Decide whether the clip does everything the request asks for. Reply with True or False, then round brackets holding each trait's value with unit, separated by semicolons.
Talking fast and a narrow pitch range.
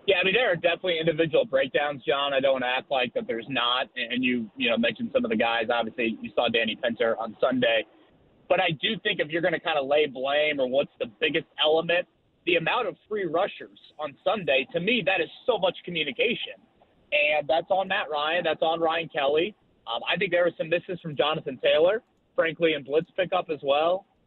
False (220 wpm; 4.9 semitones)